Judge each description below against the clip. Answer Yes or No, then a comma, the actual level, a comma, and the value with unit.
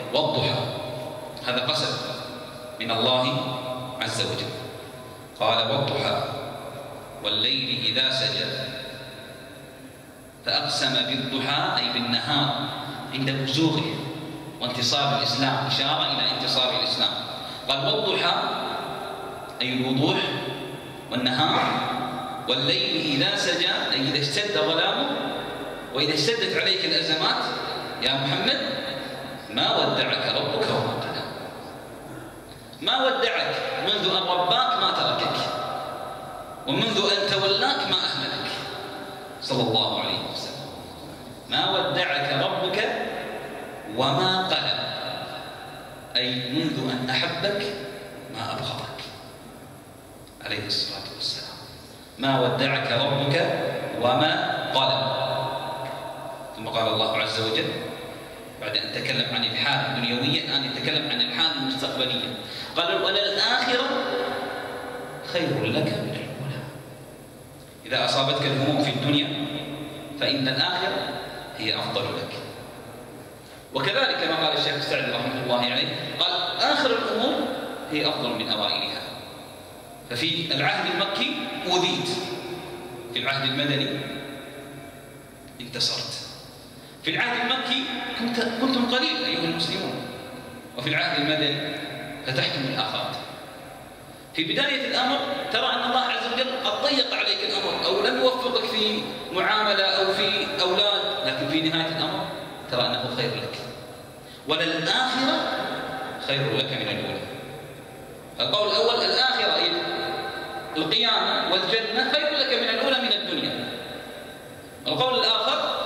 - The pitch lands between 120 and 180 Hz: Yes, medium, 140 Hz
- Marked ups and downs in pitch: Yes, wide, 6.2 semitones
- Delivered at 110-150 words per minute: No, average, 100 wpm